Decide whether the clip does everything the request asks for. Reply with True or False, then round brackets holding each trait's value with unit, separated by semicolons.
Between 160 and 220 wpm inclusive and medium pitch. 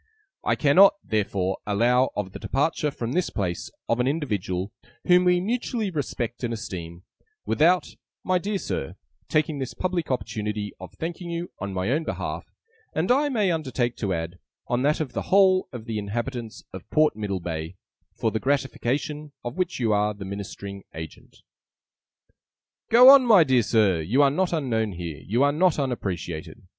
False (170 wpm; 125 Hz)